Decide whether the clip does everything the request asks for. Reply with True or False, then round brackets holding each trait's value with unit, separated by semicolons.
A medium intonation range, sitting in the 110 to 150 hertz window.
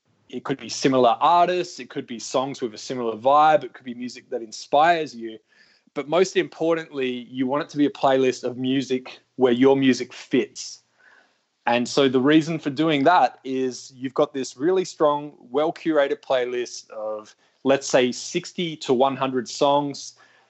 True (3.5 semitones; 135 Hz)